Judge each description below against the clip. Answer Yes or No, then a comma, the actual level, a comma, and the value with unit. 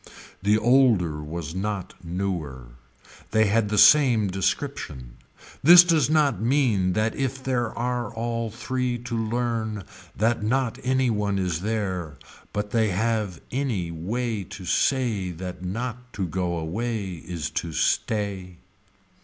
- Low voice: Yes, low, 110 Hz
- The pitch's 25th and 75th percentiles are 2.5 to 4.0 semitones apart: No, average, 4.7 semitones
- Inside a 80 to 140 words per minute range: Yes, slow, 135 wpm